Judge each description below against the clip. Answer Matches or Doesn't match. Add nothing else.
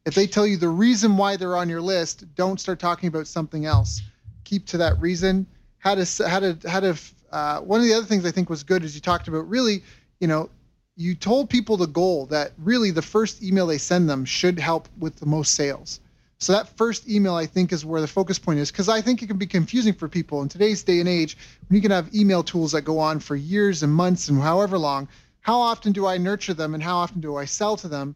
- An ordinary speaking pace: Doesn't match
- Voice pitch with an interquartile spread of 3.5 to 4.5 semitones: Matches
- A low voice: Doesn't match